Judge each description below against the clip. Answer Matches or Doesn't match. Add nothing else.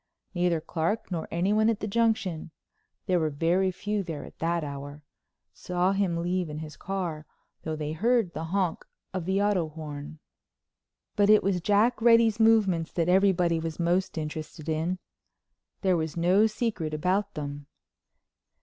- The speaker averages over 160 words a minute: Doesn't match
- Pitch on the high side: Doesn't match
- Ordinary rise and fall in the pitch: Matches